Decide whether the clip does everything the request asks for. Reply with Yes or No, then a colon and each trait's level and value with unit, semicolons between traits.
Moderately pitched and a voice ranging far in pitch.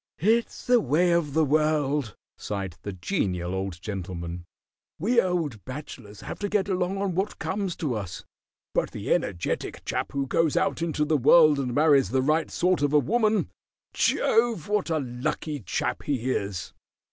Yes: medium, 150 Hz; wide, 8.1 semitones